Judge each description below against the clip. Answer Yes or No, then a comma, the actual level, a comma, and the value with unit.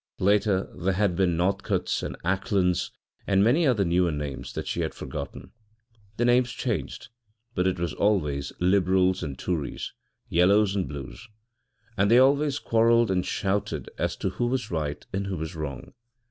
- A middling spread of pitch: Yes, average, 3.8 semitones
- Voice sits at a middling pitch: No, very low, 95 Hz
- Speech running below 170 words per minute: Yes, average, 160 wpm